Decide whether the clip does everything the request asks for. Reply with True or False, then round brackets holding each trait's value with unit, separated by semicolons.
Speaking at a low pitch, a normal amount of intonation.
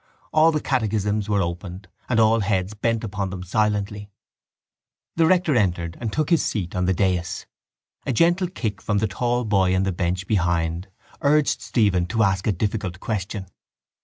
True (105 Hz; 3.5 semitones)